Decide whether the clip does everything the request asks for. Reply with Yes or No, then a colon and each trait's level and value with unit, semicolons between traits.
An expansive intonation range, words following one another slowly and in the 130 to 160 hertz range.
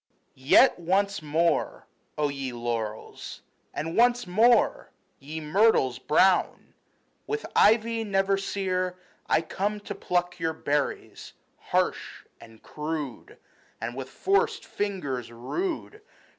No: wide, 6.3 semitones; slow, 110 wpm; medium, 175 Hz